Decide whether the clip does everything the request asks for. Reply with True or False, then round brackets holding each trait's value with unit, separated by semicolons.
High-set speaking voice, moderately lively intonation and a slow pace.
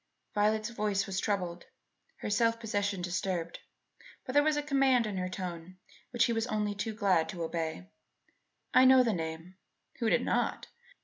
False (205 Hz; 4.1 semitones; 170 wpm)